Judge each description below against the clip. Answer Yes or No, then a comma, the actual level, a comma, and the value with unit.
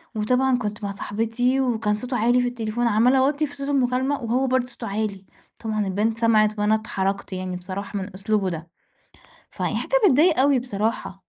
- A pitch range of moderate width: Yes, average, 3.6 semitones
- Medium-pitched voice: No, high, 225 Hz